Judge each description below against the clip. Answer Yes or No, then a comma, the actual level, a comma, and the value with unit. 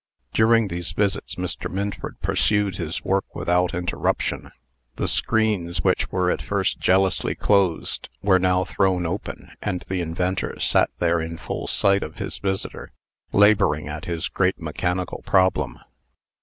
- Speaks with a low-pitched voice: Yes, very low, 90 Hz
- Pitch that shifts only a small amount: Yes, narrow, 2.1 semitones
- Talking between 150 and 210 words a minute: No, average, 140 wpm